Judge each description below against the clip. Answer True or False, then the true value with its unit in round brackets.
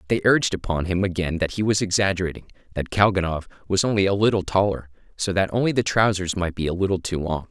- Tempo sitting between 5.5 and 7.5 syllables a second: True (6.4 syllables/s)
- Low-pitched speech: True (95 Hz)